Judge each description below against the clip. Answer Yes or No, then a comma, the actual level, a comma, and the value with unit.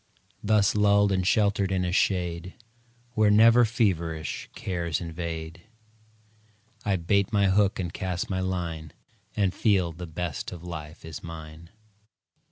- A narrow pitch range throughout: No, average, 3.2 semitones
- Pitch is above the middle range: No, very low, 90 Hz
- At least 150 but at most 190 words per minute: No, slow, 135 wpm